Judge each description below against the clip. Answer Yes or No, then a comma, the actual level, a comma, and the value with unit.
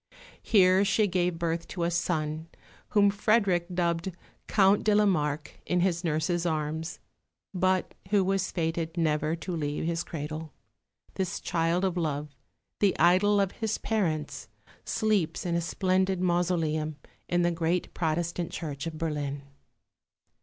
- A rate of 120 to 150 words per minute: Yes, average, 140 wpm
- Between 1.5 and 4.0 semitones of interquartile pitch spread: Yes, average, 2.9 semitones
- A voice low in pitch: No, medium, 170 Hz